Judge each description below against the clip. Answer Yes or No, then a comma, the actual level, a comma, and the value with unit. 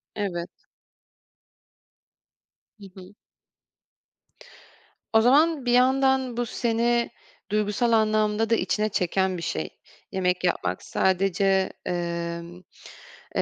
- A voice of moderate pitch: No, high, 205 Hz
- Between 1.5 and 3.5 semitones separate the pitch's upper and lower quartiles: No, average, 4.6 semitones